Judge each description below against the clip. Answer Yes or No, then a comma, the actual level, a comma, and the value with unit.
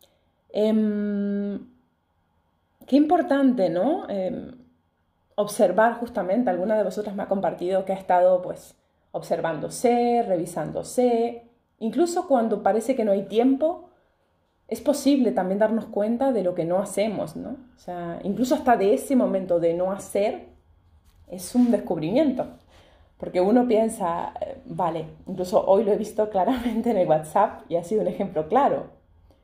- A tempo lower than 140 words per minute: No, average, 145 wpm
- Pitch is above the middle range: Yes, high, 205 Hz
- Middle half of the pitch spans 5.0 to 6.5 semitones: Yes, wide, 5.5 semitones